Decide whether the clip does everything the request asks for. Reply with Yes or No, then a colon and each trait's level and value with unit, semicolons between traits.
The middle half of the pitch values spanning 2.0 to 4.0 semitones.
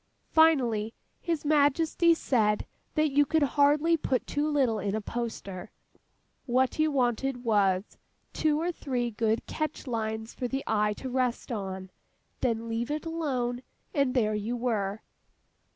No: average, 4.9 semitones